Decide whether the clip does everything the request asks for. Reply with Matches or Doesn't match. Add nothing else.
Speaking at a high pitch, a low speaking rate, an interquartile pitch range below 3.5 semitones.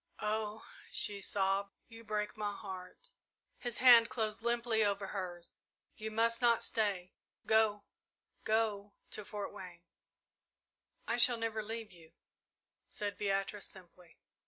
Matches